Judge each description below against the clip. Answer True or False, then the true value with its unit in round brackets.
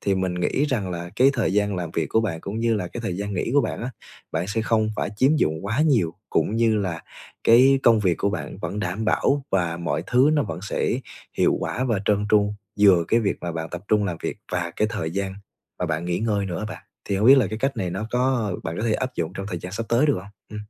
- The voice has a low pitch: True (105 Hz)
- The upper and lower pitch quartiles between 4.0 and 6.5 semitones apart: True (4.4 semitones)